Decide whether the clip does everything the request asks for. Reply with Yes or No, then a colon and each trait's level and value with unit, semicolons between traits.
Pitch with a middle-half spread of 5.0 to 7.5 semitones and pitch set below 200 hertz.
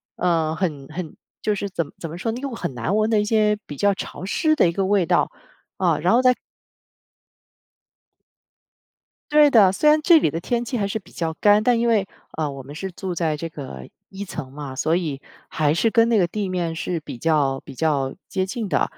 Yes: wide, 5.5 semitones; medium, 185 Hz